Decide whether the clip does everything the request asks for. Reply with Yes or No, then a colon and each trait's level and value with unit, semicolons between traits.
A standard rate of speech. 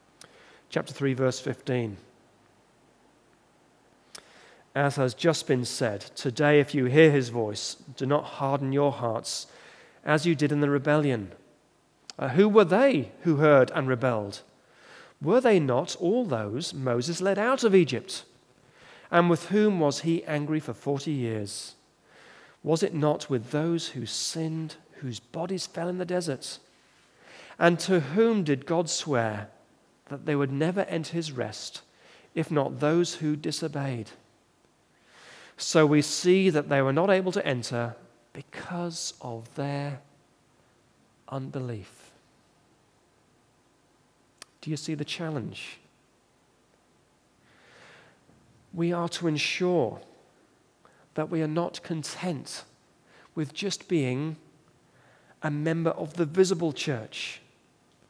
No: slow, 125 wpm